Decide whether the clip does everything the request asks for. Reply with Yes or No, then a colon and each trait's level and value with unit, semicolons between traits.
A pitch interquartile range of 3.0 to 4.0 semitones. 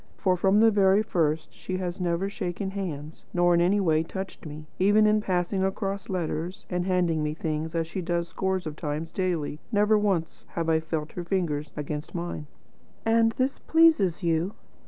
Yes: average, 3.3 semitones